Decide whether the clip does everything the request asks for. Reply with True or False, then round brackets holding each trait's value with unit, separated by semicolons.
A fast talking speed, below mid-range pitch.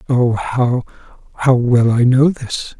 False (130 wpm; 125 Hz)